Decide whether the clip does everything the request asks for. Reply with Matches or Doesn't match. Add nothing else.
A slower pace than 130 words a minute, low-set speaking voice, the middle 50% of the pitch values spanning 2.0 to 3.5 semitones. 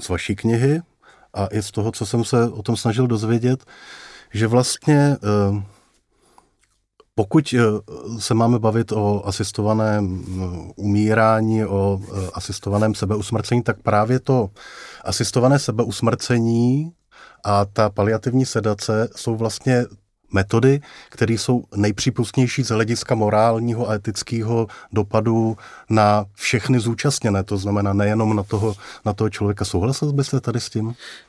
Matches